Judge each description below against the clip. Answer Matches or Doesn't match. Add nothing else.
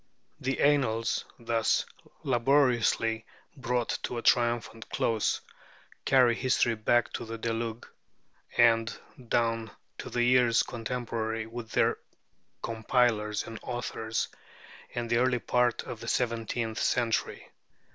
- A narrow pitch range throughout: Matches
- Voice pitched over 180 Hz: Doesn't match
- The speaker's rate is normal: Doesn't match